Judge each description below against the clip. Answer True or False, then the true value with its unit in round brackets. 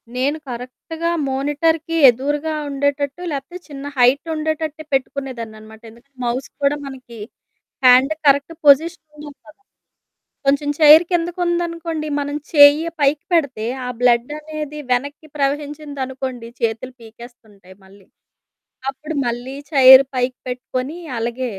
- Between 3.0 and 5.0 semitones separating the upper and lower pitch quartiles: True (3.4 semitones)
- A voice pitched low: False (280 Hz)